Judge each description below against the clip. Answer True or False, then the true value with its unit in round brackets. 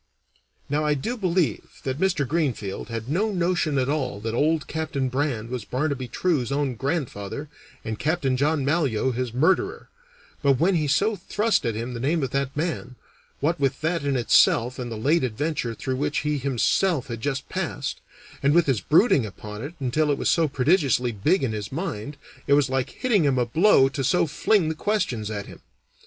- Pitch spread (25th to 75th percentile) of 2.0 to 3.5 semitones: False (4.4 semitones)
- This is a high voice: False (140 Hz)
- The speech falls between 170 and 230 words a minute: True (195 wpm)